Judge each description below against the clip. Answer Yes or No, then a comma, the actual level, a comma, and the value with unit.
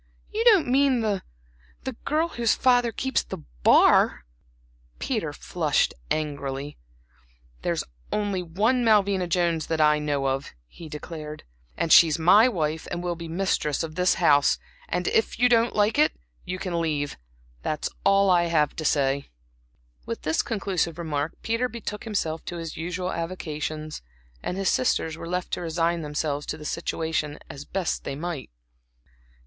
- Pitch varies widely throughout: No, average, 4.9 semitones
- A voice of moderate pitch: Yes, medium, 170 Hz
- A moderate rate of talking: Yes, average, 160 wpm